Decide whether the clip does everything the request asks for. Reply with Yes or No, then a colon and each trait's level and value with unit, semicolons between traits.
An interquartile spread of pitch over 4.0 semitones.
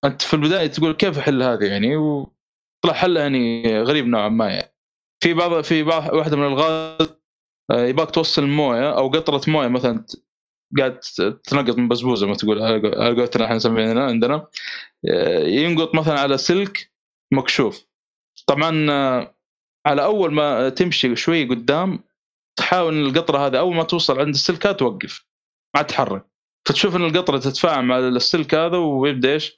Yes: average, 4.4 semitones